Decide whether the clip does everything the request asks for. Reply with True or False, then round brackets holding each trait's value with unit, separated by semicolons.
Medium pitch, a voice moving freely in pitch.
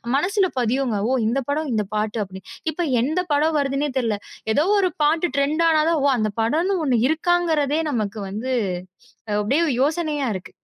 False (285 Hz; 5.8 semitones)